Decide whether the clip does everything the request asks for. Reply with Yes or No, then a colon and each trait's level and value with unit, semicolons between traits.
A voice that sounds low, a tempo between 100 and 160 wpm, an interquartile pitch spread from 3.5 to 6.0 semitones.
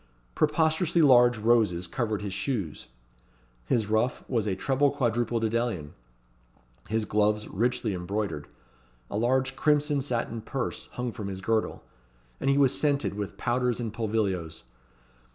Yes: low, 115 Hz; slow, 135 wpm; average, 3.9 semitones